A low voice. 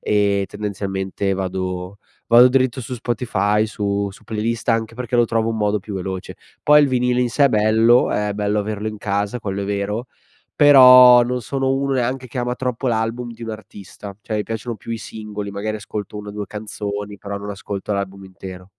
Yes: low, 105 Hz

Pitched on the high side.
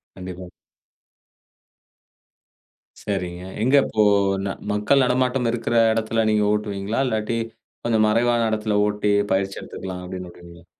No: low, 105 Hz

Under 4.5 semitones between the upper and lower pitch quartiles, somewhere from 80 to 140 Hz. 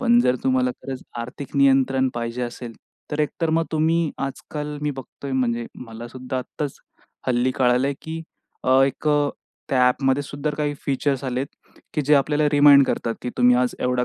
Yes: average, 2.7 semitones; low, 135 Hz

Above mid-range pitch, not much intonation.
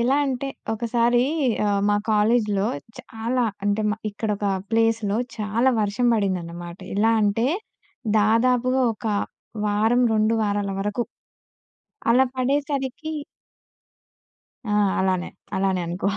No: high, 220 Hz; average, 3.1 semitones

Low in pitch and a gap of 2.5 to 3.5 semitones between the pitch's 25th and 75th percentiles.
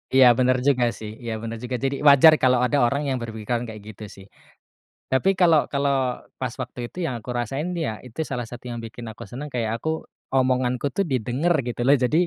Yes: low, 125 Hz; average, 2.9 semitones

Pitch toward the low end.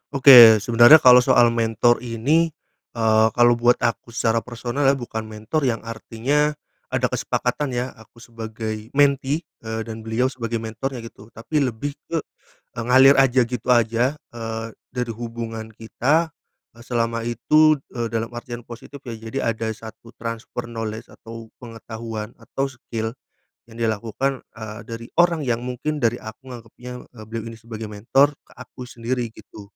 Yes: low, 115 Hz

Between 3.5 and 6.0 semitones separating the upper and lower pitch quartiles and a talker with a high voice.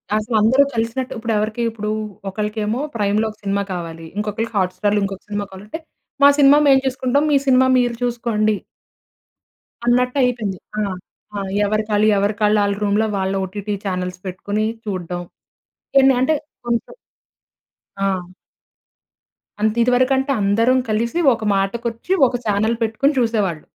No: average, 3.1 semitones; high, 215 Hz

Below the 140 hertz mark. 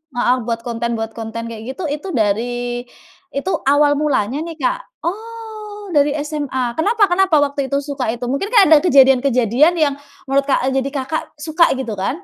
No: very high, 280 Hz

